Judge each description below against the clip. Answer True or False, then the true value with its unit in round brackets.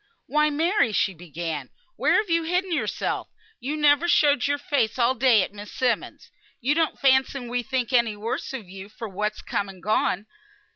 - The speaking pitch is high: True (245 Hz)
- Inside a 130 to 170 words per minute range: False (190 wpm)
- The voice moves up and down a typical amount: False (5.7 semitones)